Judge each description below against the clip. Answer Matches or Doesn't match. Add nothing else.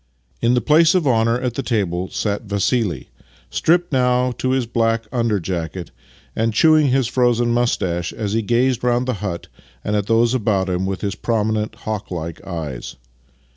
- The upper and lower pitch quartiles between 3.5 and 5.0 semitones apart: Matches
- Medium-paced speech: Matches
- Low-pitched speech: Matches